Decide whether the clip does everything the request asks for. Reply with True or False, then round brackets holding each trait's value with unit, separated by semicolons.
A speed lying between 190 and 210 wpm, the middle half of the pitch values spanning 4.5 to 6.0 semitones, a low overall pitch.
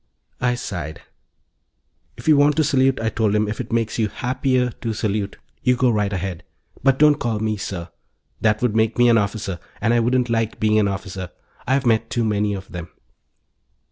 False (195 wpm; 3.2 semitones; 110 Hz)